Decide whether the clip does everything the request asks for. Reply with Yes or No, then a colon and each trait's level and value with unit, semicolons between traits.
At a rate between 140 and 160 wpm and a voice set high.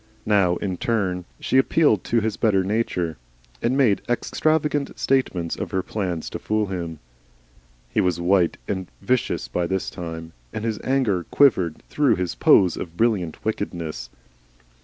No: average, 150 wpm; very low, 95 Hz